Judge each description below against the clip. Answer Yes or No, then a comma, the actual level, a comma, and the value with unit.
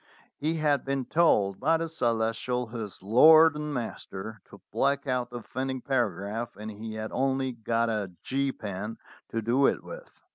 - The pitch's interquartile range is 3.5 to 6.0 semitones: Yes, average, 4.1 semitones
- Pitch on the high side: No, low, 125 Hz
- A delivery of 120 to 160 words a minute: No, average, 170 wpm